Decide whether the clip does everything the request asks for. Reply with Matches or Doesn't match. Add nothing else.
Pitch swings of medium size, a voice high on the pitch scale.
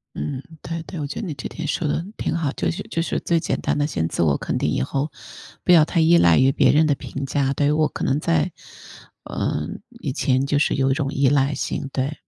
Doesn't match